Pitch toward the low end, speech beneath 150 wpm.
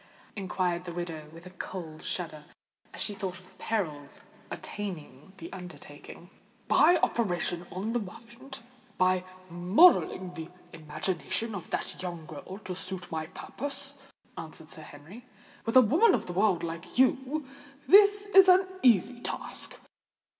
No: medium, 185 Hz; average, 140 wpm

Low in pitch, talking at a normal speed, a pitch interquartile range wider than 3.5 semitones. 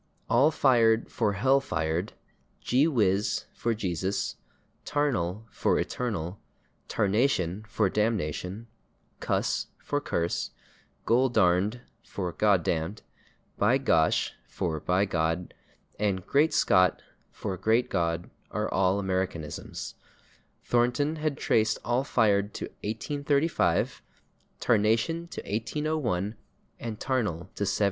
No: low, 105 Hz; slow, 105 wpm; average, 5.2 semitones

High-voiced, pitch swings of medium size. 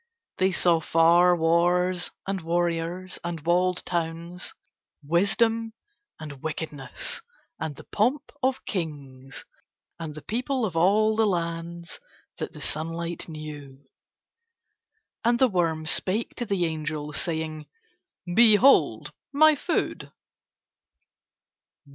No: medium, 170 Hz; average, 3.9 semitones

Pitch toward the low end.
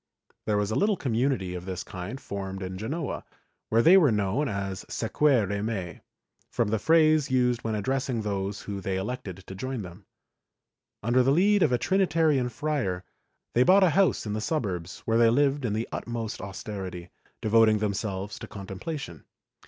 Yes: low, 110 Hz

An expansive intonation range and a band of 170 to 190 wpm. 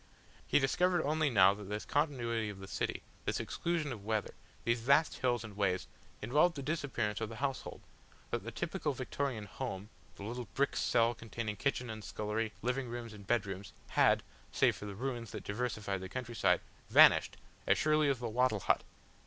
No: average, 4.3 semitones; average, 180 wpm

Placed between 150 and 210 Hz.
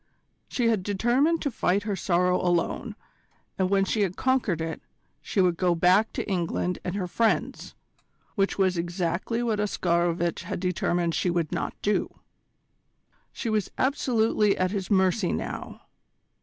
Yes: high, 190 Hz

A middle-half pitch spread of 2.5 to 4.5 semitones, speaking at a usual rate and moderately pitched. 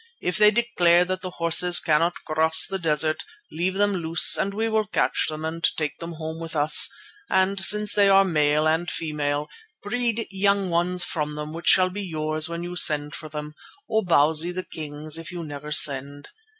Yes: average, 3.5 semitones; average, 190 wpm; medium, 165 Hz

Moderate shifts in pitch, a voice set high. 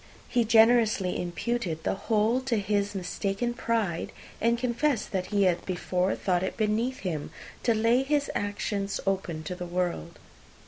Yes: average, 4.3 semitones; high, 205 Hz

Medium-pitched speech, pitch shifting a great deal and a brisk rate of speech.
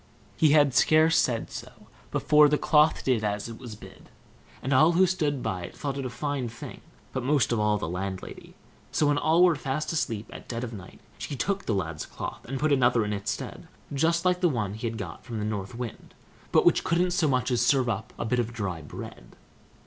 No: low, 125 Hz; wide, 5.8 semitones; fast, 225 wpm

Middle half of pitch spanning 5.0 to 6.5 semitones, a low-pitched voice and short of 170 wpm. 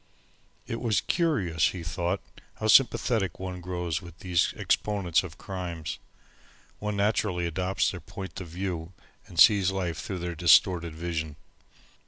No: narrow, 2.5 semitones; very low, 90 Hz; average, 140 wpm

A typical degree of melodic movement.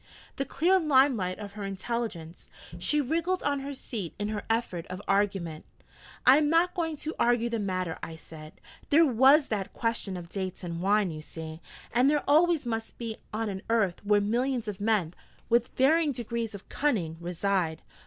No: wide, 6.5 semitones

